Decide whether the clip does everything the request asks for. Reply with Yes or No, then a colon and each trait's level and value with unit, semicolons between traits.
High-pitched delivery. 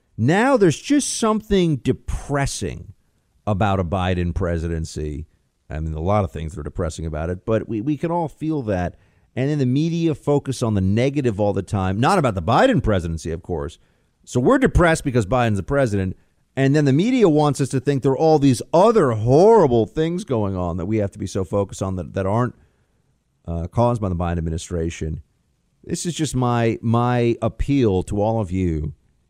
No: low, 105 Hz